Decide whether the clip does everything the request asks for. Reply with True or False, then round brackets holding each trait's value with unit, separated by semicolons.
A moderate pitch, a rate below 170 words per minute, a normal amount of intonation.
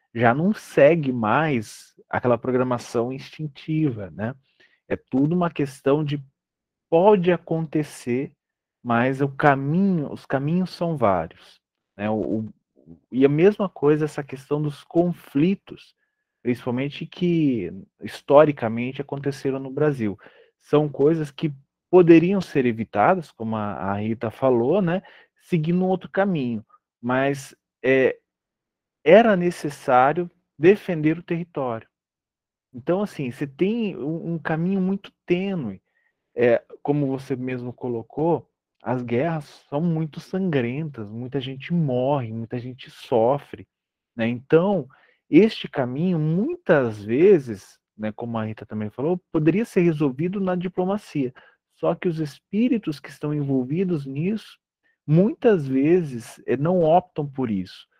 False (150 Hz; 125 wpm; 5.8 semitones)